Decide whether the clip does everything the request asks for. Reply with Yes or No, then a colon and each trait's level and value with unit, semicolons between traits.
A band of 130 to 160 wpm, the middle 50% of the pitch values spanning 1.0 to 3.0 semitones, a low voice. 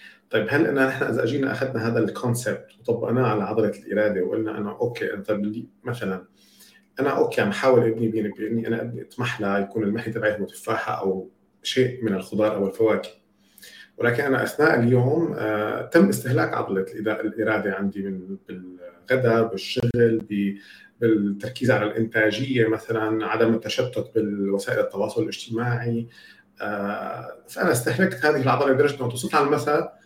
Yes: fast, 135 wpm; narrow, 2.6 semitones; low, 110 Hz